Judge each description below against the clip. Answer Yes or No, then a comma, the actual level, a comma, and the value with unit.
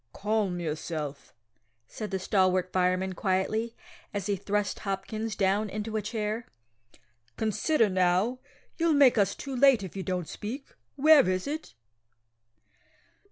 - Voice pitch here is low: No, high, 205 Hz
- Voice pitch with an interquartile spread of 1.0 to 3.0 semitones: No, average, 3.4 semitones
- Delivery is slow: Yes, slow, 130 wpm